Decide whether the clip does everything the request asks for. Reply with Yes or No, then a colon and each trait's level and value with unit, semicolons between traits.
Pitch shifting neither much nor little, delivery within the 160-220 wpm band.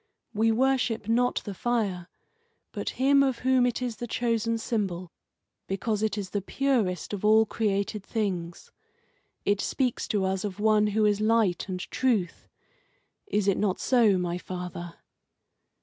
No: average, 3.6 semitones; average, 150 wpm